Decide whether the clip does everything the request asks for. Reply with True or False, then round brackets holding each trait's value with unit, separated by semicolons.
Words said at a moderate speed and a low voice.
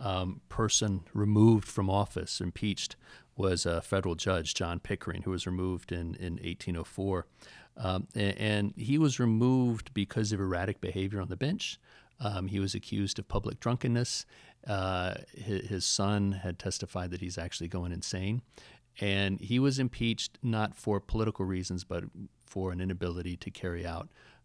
True (155 wpm; 100 Hz)